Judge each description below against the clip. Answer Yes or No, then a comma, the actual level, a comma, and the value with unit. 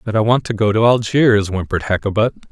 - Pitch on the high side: No, low, 110 Hz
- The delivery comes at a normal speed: No, fast, 215 wpm